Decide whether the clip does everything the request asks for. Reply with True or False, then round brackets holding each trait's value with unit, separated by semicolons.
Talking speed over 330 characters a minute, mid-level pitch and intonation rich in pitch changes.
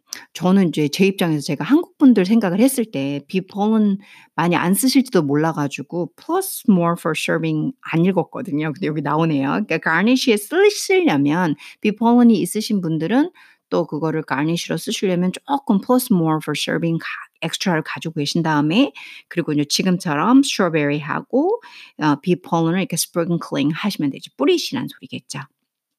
True (360 characters per minute; 175 Hz; 6.7 semitones)